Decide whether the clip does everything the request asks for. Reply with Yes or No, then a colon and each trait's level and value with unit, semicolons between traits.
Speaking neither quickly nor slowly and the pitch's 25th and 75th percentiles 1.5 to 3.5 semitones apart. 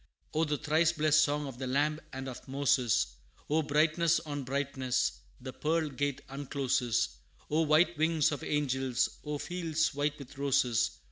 Yes: average, 155 wpm; average, 2.8 semitones